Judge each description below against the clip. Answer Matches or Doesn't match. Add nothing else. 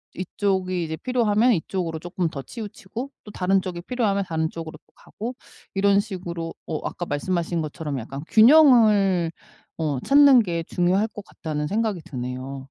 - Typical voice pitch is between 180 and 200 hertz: Matches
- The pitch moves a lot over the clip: Doesn't match